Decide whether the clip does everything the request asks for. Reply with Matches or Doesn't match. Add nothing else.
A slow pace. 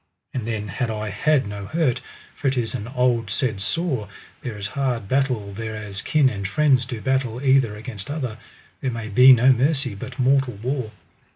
Doesn't match